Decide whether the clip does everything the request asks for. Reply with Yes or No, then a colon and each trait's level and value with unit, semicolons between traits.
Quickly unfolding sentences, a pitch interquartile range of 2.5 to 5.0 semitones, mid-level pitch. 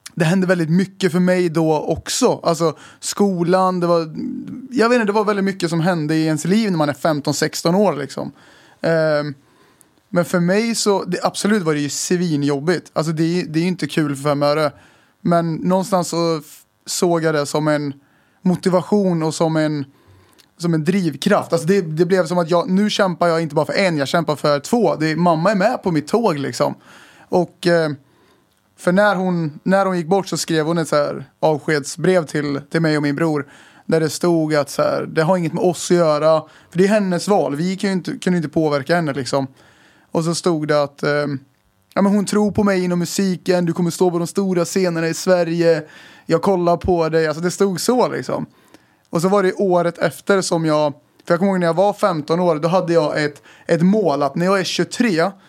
Yes: fast, 215 wpm; average, 3.3 semitones; medium, 170 Hz